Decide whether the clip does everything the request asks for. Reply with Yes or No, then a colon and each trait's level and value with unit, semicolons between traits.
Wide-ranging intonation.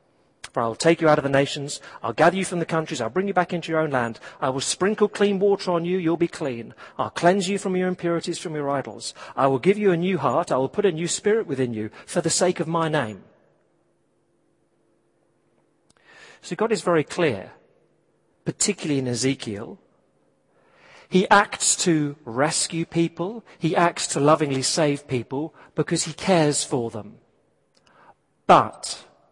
No: average, 5.0 semitones